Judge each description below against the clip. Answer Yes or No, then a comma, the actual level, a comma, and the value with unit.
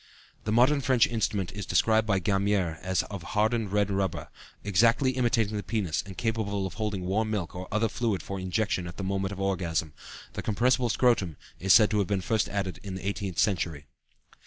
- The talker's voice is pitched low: Yes, low, 100 Hz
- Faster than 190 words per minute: Yes, average, 200 wpm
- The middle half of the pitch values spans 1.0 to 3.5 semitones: Yes, average, 2.9 semitones